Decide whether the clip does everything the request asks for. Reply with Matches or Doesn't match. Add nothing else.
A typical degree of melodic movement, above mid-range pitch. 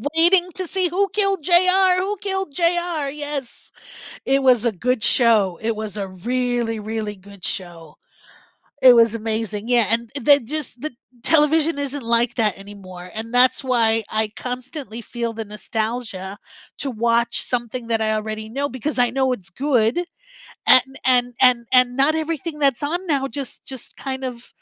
Matches